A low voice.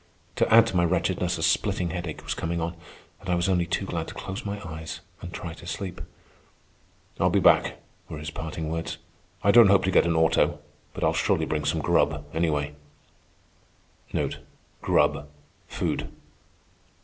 Yes: very low, 85 Hz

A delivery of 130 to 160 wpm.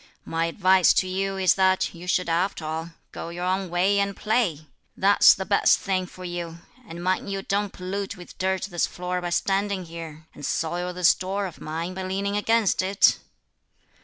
No: average, 190 wpm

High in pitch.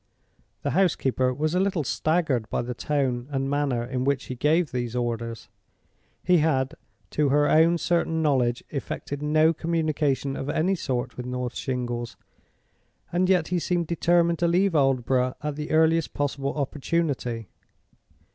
No: medium, 145 Hz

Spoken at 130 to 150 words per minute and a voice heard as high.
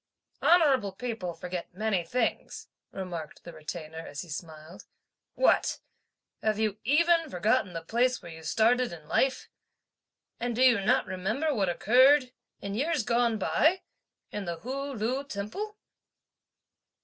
Yes: slow, 135 wpm; high, 220 Hz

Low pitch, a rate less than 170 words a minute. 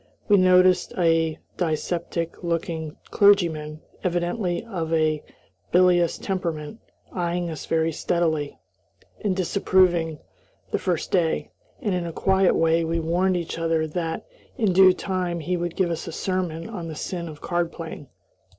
No: medium, 170 Hz; average, 145 wpm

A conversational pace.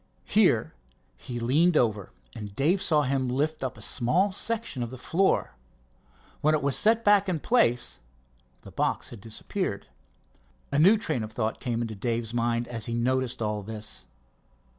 Yes: average, 165 wpm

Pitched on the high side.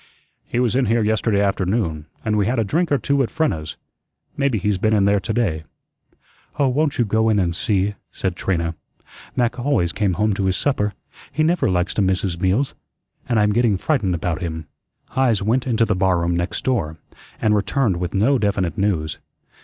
No: low, 105 Hz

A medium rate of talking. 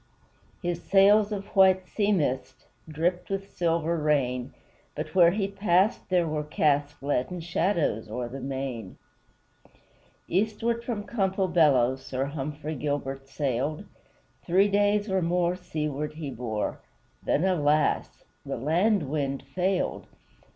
No: slow, 125 wpm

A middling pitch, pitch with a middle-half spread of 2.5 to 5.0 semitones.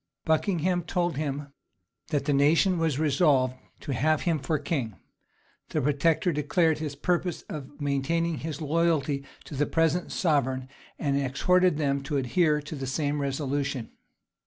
Yes: medium, 150 Hz; average, 2.9 semitones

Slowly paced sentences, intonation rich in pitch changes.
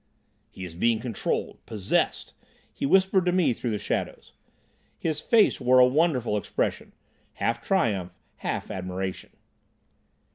Yes: slow, 120 wpm; wide, 8.5 semitones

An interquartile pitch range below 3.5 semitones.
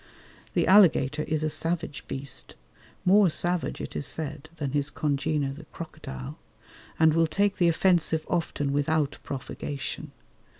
Yes: average, 2.9 semitones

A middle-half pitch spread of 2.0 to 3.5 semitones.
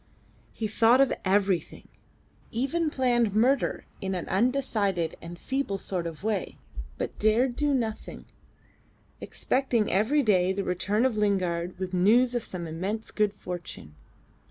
No: average, 4.8 semitones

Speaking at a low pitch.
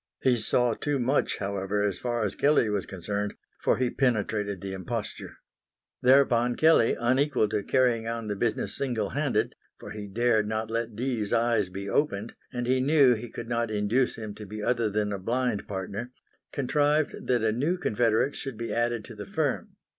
Yes: low, 115 Hz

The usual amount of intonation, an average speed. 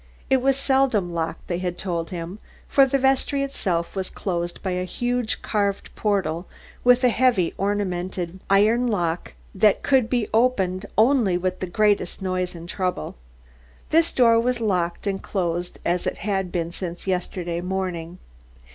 Yes: average, 4.7 semitones; average, 155 wpm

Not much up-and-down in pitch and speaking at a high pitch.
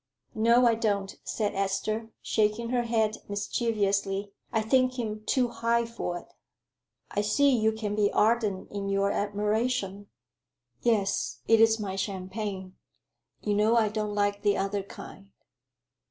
Yes: narrow, 2.3 semitones; high, 210 Hz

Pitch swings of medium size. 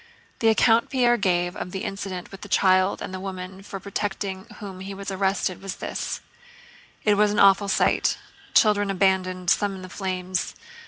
No: narrow, 1.5 semitones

